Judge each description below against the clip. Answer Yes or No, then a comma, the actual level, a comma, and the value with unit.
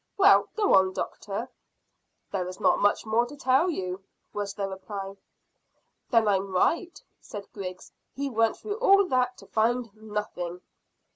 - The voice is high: Yes, high, 215 Hz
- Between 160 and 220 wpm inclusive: No, average, 150 wpm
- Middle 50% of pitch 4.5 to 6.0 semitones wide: Yes, average, 4.8 semitones